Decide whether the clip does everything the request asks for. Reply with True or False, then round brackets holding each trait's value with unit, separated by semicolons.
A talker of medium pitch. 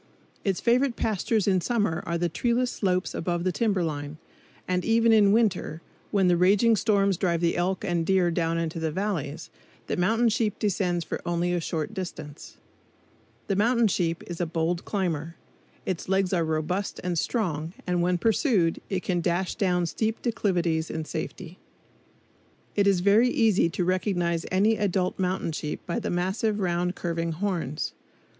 True (180 Hz)